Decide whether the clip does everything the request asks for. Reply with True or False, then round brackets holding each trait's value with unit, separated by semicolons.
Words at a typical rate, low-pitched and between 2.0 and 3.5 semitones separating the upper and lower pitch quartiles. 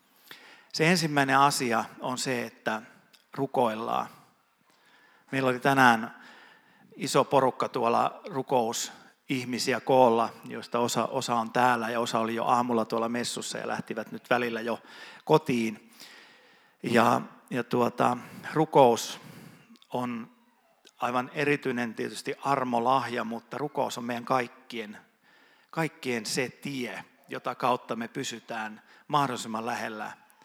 True (110 wpm; 125 Hz; 3.1 semitones)